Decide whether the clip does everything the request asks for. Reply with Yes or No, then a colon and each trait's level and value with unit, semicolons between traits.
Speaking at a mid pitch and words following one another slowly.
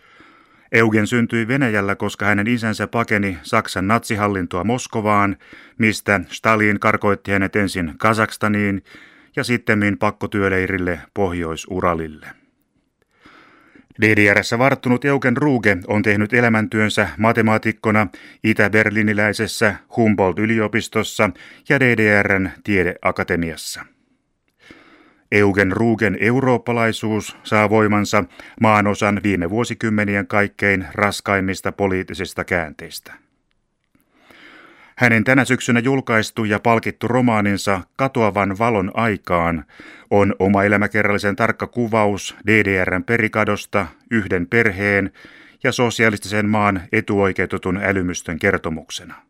No: low, 105 Hz; slow, 85 wpm